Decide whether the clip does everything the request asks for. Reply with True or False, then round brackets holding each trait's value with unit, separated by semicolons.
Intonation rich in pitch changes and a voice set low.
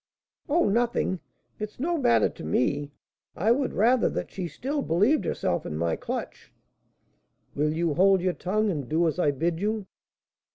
False (6.8 semitones; 185 Hz)